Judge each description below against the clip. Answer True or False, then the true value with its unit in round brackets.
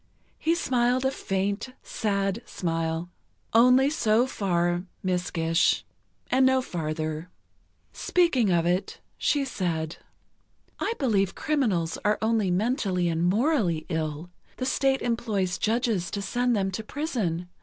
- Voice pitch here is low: False (200 Hz)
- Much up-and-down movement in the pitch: True (6.1 semitones)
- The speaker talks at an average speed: False (125 wpm)